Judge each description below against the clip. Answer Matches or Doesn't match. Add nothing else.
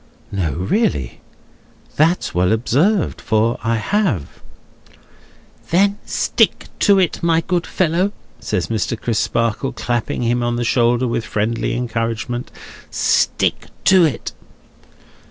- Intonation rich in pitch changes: Matches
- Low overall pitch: Matches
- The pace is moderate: Doesn't match